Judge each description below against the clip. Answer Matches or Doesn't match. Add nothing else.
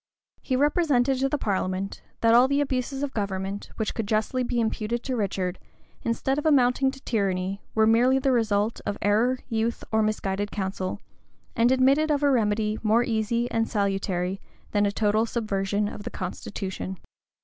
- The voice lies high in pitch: Matches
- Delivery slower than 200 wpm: Matches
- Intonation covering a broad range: Doesn't match